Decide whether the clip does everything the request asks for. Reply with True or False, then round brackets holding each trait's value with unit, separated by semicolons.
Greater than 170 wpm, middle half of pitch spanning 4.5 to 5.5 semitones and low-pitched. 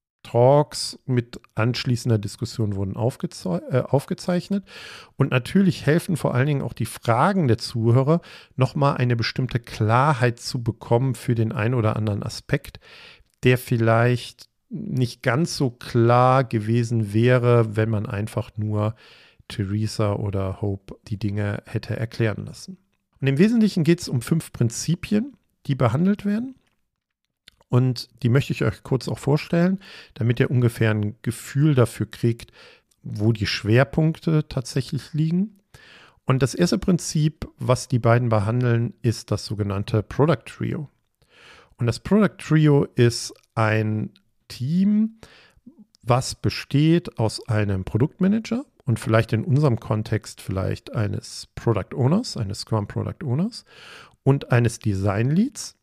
False (135 wpm; 5.1 semitones; 120 Hz)